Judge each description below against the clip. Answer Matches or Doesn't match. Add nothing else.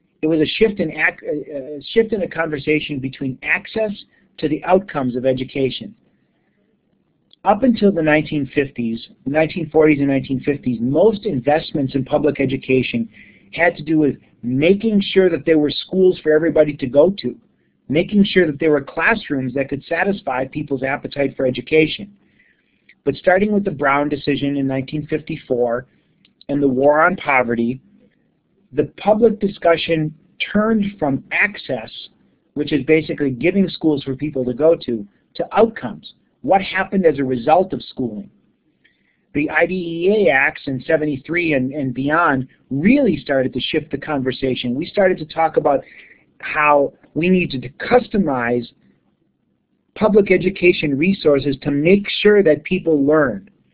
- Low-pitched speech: Doesn't match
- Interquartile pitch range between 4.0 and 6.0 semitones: Matches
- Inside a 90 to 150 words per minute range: Matches